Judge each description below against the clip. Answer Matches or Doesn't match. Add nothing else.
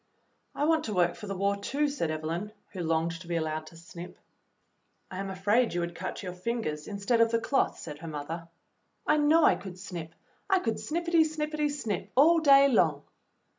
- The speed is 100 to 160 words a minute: Doesn't match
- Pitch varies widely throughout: Matches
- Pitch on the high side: Matches